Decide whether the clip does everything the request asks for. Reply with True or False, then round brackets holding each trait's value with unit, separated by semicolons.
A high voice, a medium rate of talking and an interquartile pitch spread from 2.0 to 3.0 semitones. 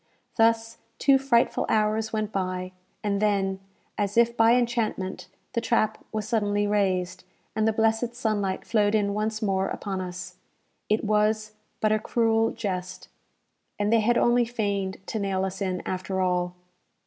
True (210 Hz; 155 wpm; 2.7 semitones)